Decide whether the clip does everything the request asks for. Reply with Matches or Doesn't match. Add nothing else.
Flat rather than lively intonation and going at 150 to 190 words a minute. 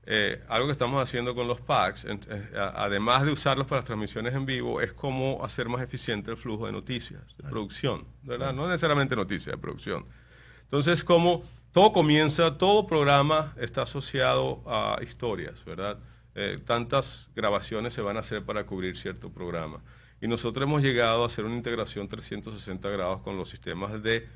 Doesn't match